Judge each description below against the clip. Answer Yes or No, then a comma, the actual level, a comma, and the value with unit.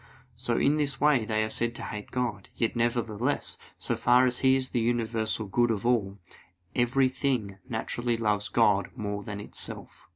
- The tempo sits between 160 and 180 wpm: Yes, average, 175 wpm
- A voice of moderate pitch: No, low, 115 Hz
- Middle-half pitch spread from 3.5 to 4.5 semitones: No, average, 2.8 semitones